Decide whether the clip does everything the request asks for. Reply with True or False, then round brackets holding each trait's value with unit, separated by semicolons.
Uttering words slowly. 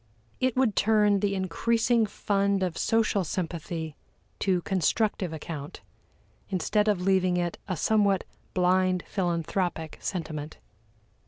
True (110 wpm)